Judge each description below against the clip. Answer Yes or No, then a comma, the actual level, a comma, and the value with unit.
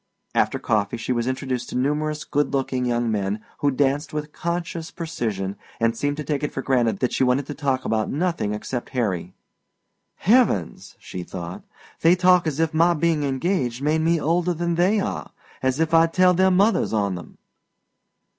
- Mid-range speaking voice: Yes, medium, 145 Hz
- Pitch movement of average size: No, wide, 5.7 semitones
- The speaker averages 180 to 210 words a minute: Yes, average, 185 wpm